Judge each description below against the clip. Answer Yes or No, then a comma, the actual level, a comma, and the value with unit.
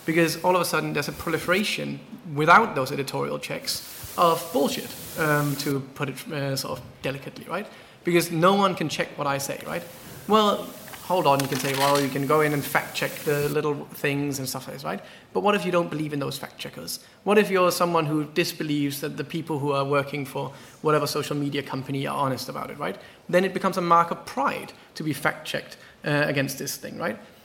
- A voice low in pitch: No, medium, 150 Hz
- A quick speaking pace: Yes, fast, 225 wpm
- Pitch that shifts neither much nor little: Yes, average, 3.5 semitones